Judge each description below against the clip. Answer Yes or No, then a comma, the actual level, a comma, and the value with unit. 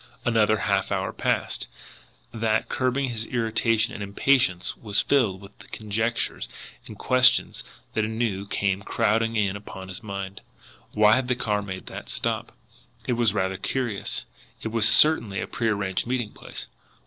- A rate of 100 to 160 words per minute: Yes, average, 150 wpm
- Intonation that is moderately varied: Yes, average, 3.0 semitones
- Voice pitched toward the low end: Yes, low, 110 Hz